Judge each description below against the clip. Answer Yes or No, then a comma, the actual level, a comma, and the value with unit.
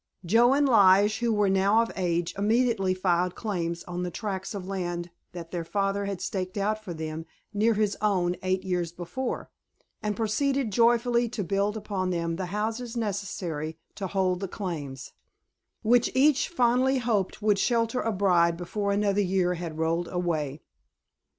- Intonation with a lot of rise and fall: No, average, 3.7 semitones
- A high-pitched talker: Yes, high, 195 Hz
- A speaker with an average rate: Yes, average, 165 wpm